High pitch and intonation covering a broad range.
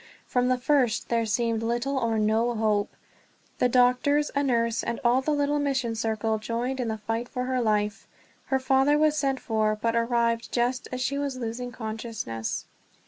No: high, 240 Hz; average, 2.7 semitones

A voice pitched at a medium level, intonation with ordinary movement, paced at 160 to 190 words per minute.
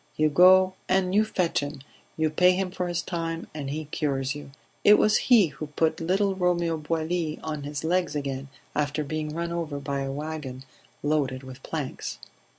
Yes: medium, 155 Hz; average, 3.6 semitones; average, 180 wpm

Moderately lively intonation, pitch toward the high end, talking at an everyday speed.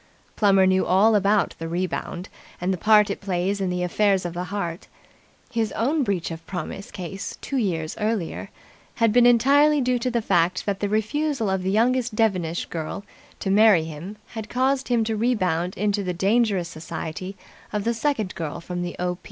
Yes: average, 4.0 semitones; high, 200 Hz; average, 185 wpm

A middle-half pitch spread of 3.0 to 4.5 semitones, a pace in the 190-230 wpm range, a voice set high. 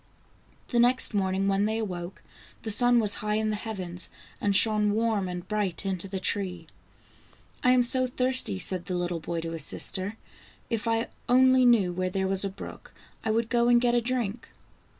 Yes: average, 4.1 semitones; average, 195 wpm; high, 210 Hz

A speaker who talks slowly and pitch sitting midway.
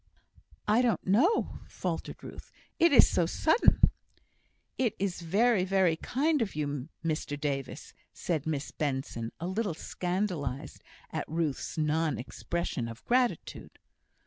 Yes: slow, 130 wpm; medium, 170 Hz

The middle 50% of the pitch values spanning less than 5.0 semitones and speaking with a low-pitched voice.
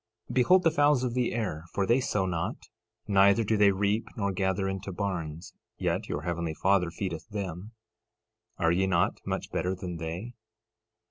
Yes: average, 3.7 semitones; very low, 95 Hz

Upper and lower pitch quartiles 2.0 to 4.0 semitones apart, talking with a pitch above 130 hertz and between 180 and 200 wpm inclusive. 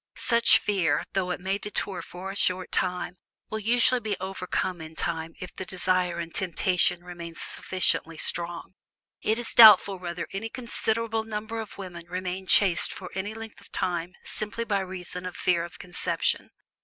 No: average, 3.0 semitones; medium, 185 Hz; average, 165 wpm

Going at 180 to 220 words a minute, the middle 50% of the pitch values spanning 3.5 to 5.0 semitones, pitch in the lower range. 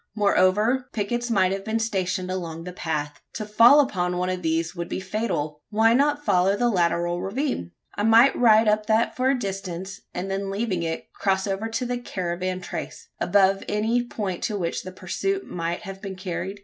No: average, 190 wpm; average, 3.9 semitones; high, 195 Hz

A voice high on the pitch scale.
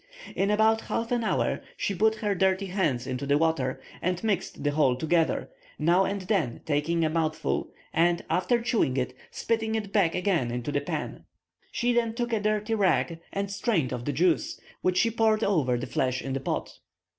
No: medium, 180 Hz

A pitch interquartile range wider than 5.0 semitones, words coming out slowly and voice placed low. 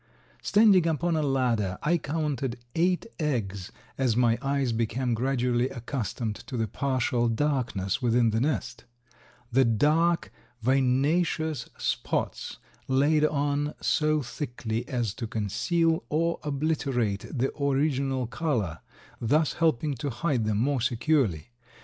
No: average, 4.5 semitones; slow, 120 wpm; low, 130 Hz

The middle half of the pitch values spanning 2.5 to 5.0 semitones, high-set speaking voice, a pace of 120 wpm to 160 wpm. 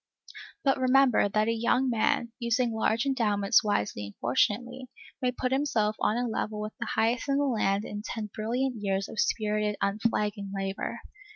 No: average, 3.2 semitones; high, 220 Hz; average, 170 wpm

